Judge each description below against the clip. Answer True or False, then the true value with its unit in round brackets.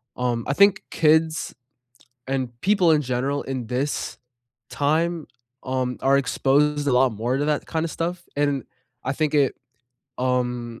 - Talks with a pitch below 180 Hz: True (140 Hz)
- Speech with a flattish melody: False (3.5 semitones)